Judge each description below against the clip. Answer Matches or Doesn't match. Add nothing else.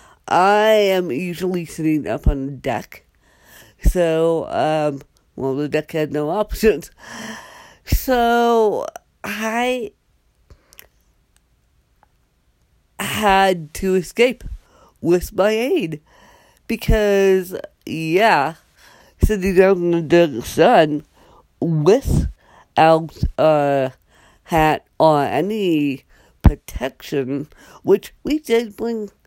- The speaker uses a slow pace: Matches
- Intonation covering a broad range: Matches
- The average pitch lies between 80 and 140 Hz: Doesn't match